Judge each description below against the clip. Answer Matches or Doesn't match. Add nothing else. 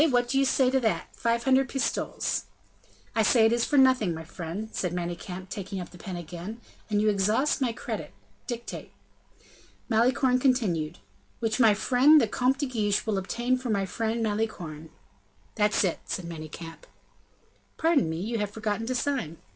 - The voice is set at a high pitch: Matches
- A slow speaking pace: Doesn't match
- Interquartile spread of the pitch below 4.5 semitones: Doesn't match